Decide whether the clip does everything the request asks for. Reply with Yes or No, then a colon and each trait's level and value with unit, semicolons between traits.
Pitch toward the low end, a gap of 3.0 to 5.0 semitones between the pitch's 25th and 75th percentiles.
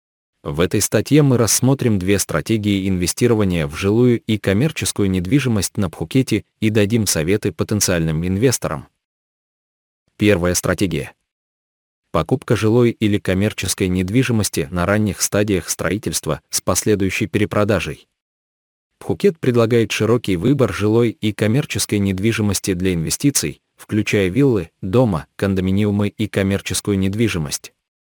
Yes: low, 105 Hz; average, 3.4 semitones